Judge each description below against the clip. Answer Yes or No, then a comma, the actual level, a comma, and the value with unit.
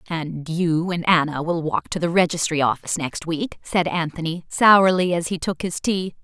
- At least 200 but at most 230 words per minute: No, average, 190 wpm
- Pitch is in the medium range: Yes, medium, 170 Hz